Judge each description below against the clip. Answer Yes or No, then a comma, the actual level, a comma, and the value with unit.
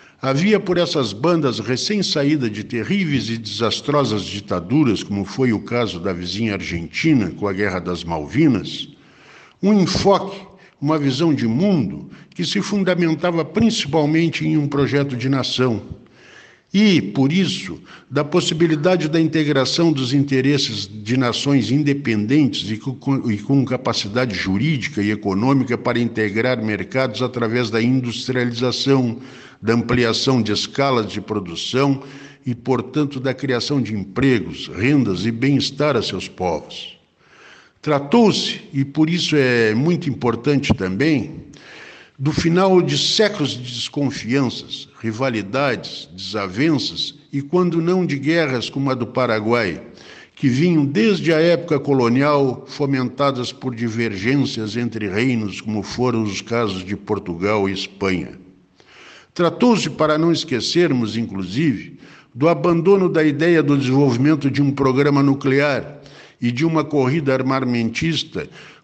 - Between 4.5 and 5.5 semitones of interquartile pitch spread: Yes, average, 4.9 semitones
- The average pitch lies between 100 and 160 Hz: Yes, low, 135 Hz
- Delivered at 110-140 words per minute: Yes, average, 125 wpm